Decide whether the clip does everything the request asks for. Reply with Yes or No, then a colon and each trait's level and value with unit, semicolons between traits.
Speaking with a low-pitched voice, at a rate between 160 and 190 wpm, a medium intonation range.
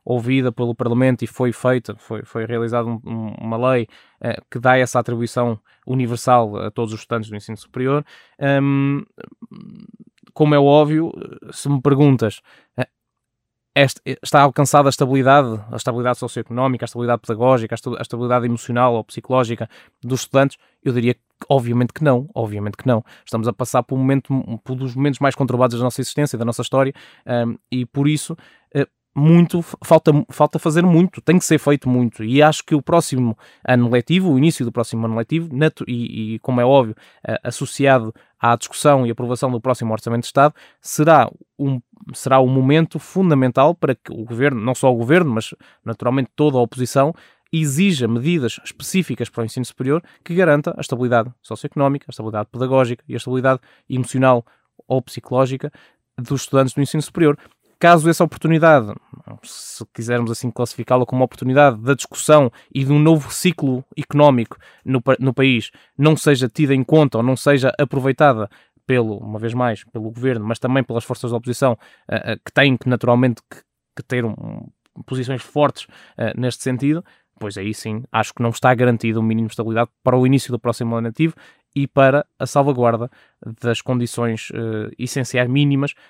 Yes: low, 130 Hz; average, 175 wpm; average, 3.2 semitones